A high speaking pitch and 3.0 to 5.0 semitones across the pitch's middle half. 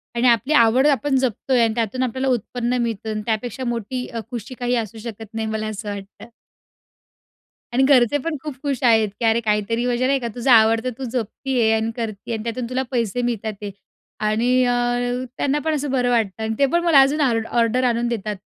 No: high, 235 Hz; narrow, 2.6 semitones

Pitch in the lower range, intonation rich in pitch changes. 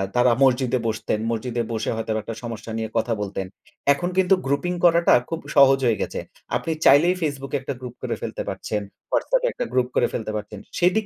Yes: low, 130 Hz; wide, 6.3 semitones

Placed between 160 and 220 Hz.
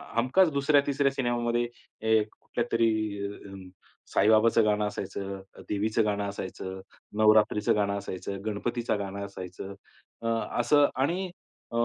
No: low, 110 Hz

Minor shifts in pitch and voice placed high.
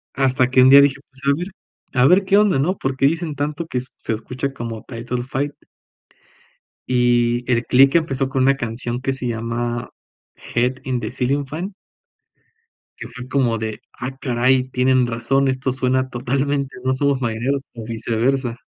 No: narrow, 2.3 semitones; low, 130 Hz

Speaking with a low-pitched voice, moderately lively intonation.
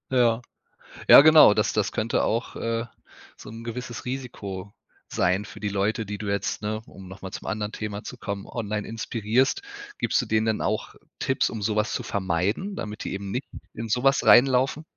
Yes: low, 110 Hz; average, 3.0 semitones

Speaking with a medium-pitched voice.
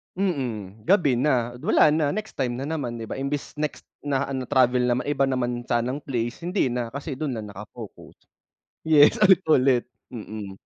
No: low, 130 Hz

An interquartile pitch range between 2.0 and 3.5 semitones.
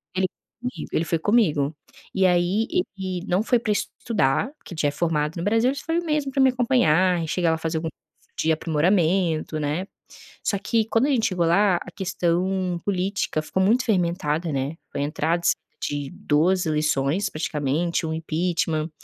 No: average, 4.3 semitones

